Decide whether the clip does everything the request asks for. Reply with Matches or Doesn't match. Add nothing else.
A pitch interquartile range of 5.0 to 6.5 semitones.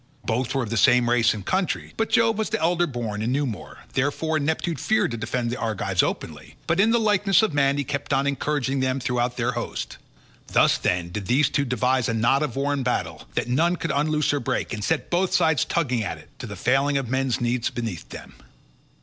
Doesn't match